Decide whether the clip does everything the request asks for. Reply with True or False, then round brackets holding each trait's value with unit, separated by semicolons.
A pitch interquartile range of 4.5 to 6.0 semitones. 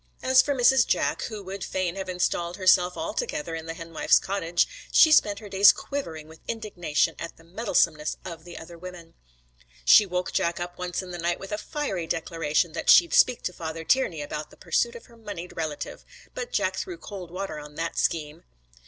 False (4.0 semitones)